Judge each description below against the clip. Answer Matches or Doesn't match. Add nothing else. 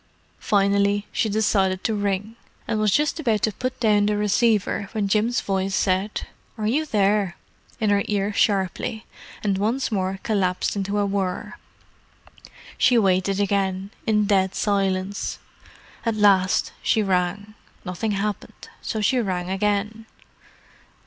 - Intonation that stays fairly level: Matches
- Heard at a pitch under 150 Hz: Doesn't match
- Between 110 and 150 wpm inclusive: Matches